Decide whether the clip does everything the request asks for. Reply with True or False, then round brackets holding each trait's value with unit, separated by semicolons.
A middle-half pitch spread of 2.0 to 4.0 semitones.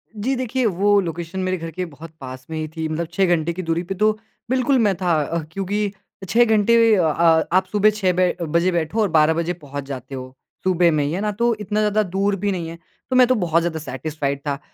False (4.5 semitones)